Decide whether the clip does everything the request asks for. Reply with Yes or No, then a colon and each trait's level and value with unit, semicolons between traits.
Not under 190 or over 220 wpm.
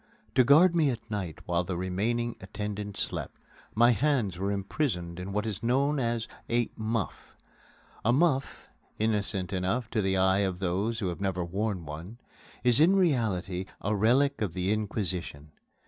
No: average, 165 wpm